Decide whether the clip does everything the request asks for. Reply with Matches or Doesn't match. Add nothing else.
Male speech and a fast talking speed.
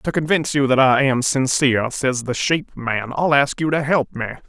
Matches